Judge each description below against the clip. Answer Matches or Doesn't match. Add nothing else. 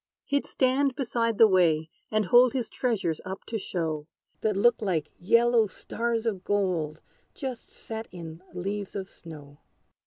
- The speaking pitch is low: Doesn't match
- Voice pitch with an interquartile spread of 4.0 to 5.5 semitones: Matches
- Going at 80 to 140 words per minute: Doesn't match